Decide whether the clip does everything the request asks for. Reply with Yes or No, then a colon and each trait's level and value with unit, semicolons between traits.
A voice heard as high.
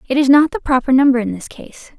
Yes: very high, 270 Hz